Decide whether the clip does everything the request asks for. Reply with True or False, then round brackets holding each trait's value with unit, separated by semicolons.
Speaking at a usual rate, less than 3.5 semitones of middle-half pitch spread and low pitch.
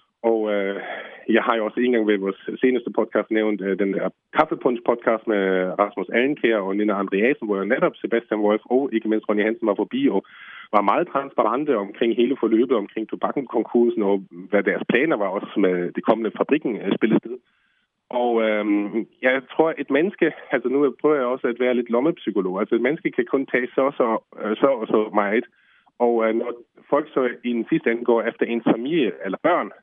True (200 wpm; 2.8 semitones; 110 Hz)